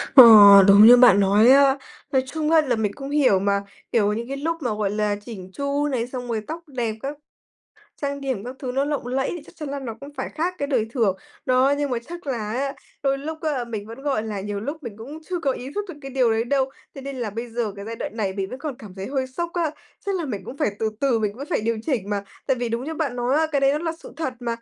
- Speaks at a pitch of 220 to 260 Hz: Yes, very high, 255 Hz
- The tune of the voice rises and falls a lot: No, average, 4.2 semitones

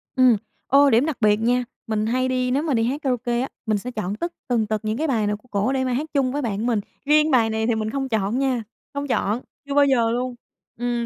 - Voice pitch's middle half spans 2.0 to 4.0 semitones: Yes, average, 3.4 semitones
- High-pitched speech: Yes, high, 245 Hz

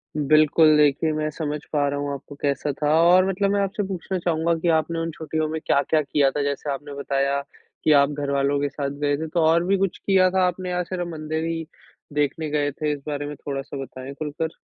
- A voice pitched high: No, medium, 155 Hz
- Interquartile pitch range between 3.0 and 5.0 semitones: No, narrow, 2.6 semitones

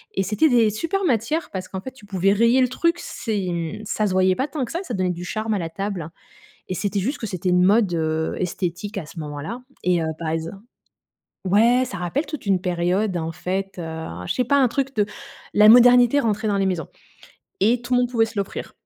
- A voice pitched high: Yes, high, 205 Hz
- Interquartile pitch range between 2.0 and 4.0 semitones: No, average, 5.2 semitones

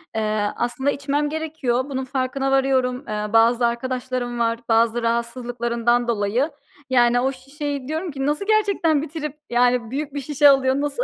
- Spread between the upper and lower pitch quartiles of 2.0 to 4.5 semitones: Yes, average, 3.2 semitones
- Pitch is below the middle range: No, very high, 260 Hz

